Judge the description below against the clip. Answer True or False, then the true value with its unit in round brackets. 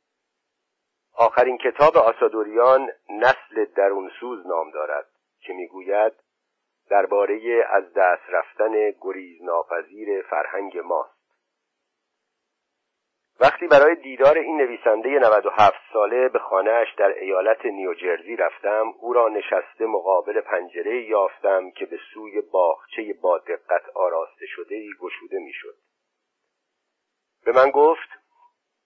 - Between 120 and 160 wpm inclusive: False (105 wpm)